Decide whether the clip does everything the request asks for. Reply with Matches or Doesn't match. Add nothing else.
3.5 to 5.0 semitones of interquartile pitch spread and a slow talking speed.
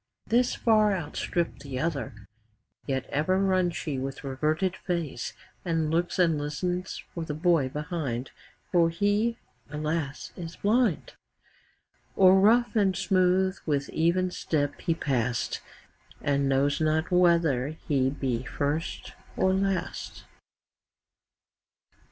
Matches